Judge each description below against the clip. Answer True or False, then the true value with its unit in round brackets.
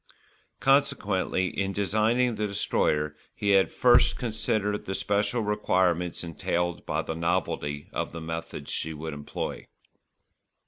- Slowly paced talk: True (125 wpm)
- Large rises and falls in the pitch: False (4.4 semitones)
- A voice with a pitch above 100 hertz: False (95 Hz)